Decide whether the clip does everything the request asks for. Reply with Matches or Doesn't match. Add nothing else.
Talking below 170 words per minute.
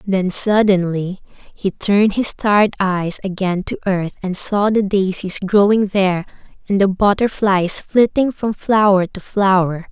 Matches